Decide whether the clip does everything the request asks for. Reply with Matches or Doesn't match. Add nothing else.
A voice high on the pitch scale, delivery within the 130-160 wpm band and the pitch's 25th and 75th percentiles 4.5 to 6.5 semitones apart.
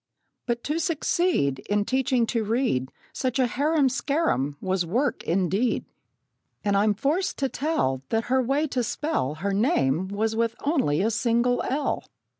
Matches